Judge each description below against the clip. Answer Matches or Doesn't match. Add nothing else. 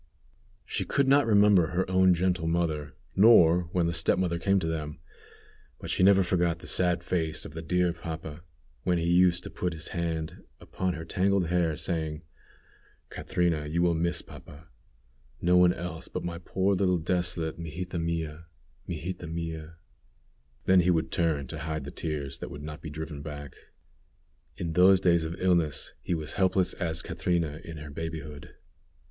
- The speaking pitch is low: Matches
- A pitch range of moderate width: Doesn't match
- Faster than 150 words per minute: Matches